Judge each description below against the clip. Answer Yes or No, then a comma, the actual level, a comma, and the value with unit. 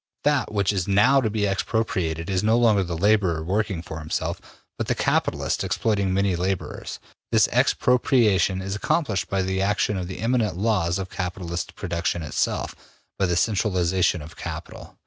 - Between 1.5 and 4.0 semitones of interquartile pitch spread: Yes, average, 3.3 semitones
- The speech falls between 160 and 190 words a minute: Yes, average, 165 wpm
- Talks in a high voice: No, very low, 95 Hz